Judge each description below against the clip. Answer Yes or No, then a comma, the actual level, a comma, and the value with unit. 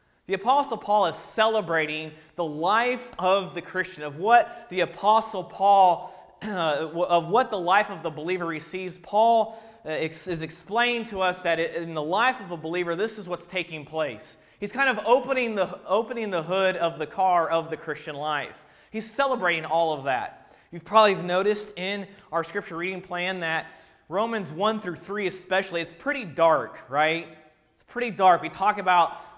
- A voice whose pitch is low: No, medium, 185 Hz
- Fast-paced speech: No, average, 175 wpm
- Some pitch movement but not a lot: Yes, average, 4.3 semitones